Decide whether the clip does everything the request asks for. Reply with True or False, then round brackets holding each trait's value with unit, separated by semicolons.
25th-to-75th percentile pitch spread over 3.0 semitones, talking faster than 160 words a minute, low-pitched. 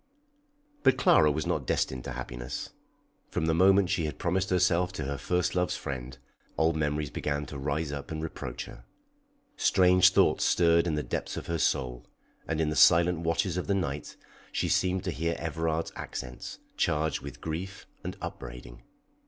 True (3.9 semitones; 175 wpm; 80 Hz)